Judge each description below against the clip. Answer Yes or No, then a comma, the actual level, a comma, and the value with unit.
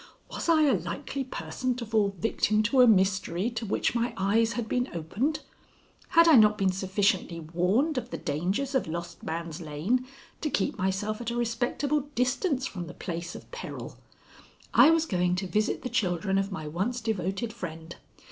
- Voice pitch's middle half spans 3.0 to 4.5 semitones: No, wide, 5.6 semitones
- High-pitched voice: Yes, high, 210 Hz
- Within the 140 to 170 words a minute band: No, average, 180 wpm